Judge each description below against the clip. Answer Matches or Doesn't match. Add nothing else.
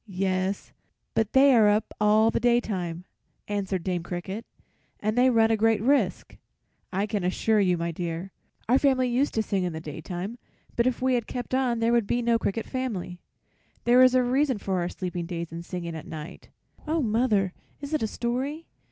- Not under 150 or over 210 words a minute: Matches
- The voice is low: Doesn't match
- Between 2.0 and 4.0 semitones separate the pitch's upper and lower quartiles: Doesn't match